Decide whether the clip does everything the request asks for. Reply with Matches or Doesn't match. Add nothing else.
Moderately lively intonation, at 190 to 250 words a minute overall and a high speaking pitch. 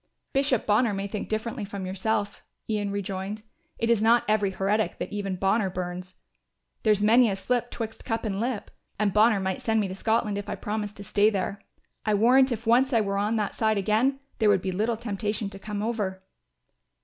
Doesn't match